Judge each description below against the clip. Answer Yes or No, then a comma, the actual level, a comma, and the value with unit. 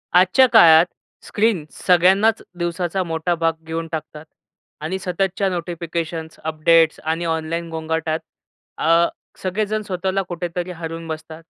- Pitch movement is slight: Yes, narrow, 2.2 semitones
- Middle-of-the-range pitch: Yes, medium, 170 Hz